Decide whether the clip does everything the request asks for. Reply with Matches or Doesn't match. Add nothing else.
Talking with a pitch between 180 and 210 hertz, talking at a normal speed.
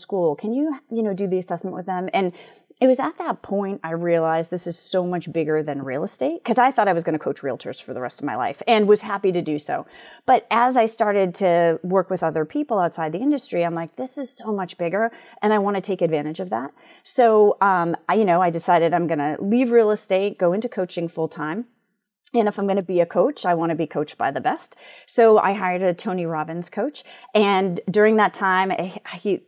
Doesn't match